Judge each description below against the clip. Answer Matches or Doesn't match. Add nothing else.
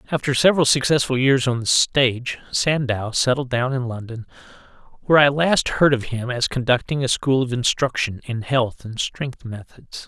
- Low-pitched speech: Matches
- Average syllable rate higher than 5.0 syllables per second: Doesn't match